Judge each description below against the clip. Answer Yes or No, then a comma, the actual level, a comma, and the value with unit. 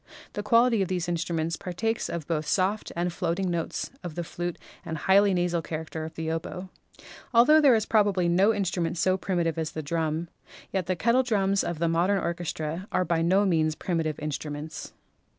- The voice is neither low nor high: Yes, medium, 175 Hz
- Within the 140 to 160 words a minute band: No, average, 190 wpm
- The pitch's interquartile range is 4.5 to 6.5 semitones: No, average, 3.1 semitones